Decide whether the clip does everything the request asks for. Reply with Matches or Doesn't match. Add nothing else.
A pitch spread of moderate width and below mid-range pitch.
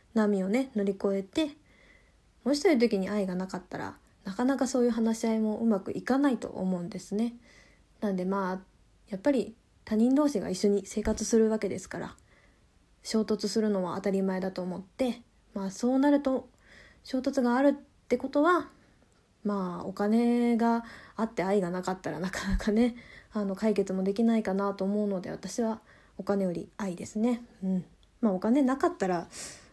Doesn't match